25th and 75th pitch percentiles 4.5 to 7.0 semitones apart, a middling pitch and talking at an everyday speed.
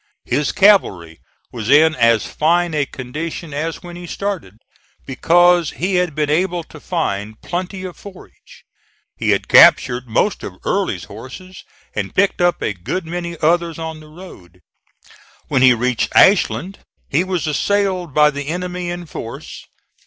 Yes: average, 5.3 semitones; medium, 165 Hz; average, 155 wpm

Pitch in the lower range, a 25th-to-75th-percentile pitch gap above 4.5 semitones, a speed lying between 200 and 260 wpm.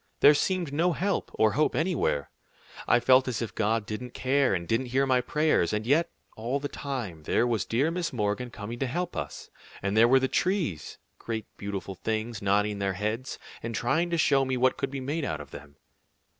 Yes: low, 125 Hz; average, 5.0 semitones; fast, 205 wpm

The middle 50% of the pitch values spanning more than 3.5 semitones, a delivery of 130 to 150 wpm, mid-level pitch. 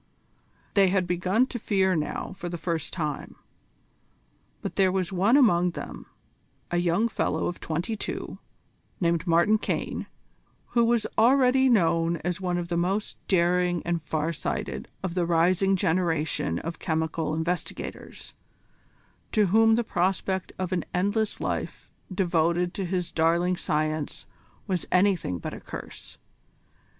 No: narrow, 2.6 semitones; average, 140 wpm; medium, 180 Hz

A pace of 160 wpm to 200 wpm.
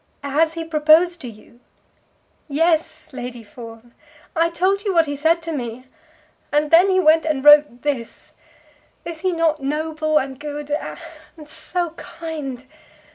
No: average, 145 wpm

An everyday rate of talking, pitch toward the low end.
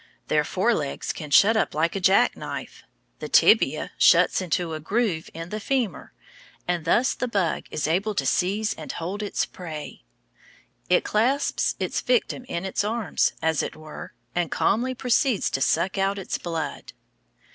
No: average, 165 wpm; medium, 185 Hz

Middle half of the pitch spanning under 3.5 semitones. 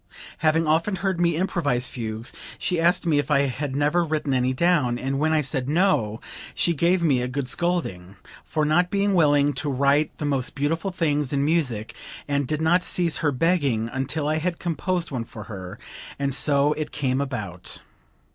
No: average, 4.2 semitones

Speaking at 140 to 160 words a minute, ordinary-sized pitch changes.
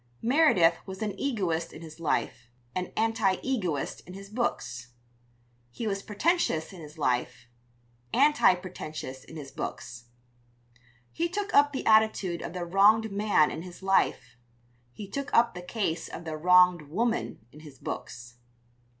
No: average, 150 wpm; wide, 6.1 semitones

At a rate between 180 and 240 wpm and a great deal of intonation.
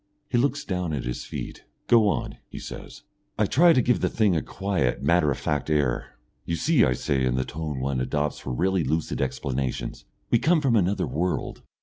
Yes: fast, 205 wpm; wide, 7.7 semitones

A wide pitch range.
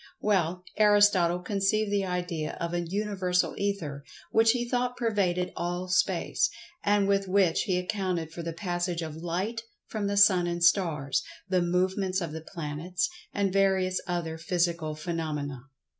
No: average, 2.9 semitones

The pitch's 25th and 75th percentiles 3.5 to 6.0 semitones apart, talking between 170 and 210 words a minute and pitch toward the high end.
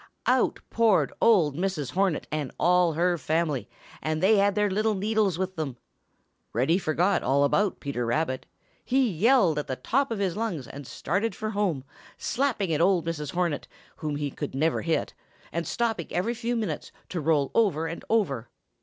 No: wide, 5.5 semitones; average, 175 wpm; medium, 175 Hz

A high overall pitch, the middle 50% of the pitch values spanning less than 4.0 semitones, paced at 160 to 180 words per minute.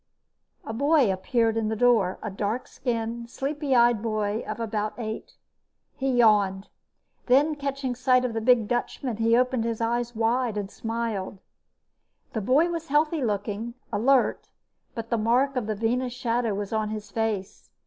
Yes: high, 230 Hz; average, 2.8 semitones; average, 165 wpm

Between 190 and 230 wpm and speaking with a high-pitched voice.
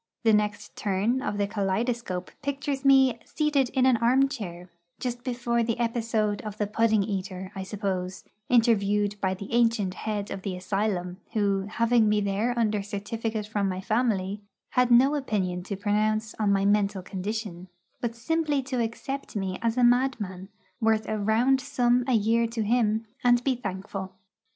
No: average, 165 wpm; high, 215 Hz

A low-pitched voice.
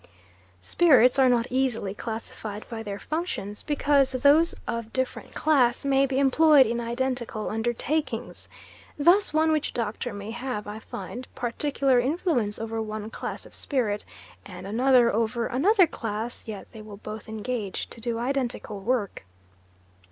No: high, 240 Hz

